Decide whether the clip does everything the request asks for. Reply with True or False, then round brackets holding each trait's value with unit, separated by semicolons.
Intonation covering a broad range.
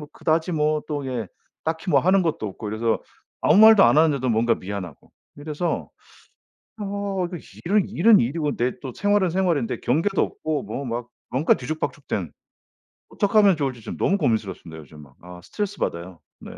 True (7.9 semitones)